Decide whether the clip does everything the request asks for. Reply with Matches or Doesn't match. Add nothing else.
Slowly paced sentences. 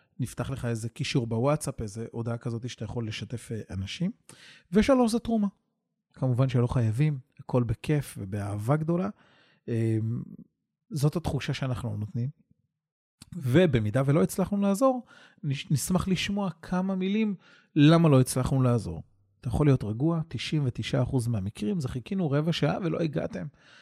Doesn't match